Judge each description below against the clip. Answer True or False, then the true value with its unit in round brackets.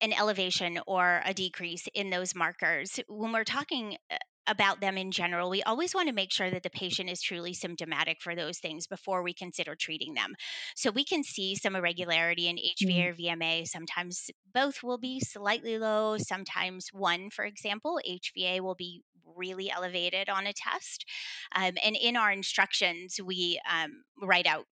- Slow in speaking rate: False (175 wpm)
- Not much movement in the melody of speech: False (3.3 semitones)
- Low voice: False (190 Hz)